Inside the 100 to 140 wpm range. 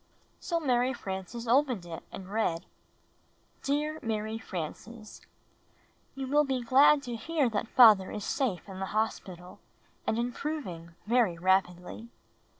Yes: slow, 135 wpm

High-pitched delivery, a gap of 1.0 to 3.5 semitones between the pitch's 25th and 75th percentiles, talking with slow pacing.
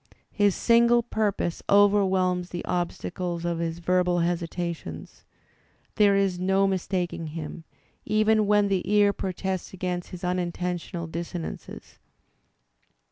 No: medium, 180 Hz; narrow, 2.5 semitones; slow, 115 wpm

